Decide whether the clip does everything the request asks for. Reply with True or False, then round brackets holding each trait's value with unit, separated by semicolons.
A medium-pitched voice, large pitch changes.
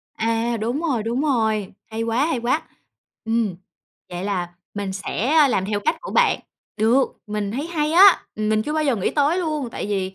False (230 Hz; 6.0 semitones)